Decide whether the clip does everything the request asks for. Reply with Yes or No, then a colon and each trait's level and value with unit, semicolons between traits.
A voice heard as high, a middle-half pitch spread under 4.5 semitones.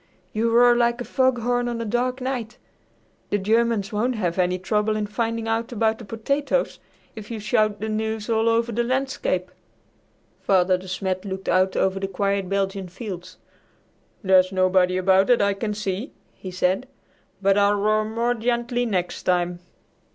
Yes: high, 215 Hz; average, 3.6 semitones